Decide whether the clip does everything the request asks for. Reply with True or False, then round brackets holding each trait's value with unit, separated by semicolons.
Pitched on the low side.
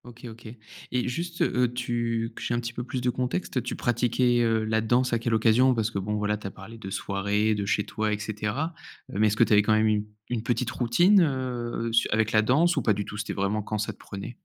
True (115 Hz)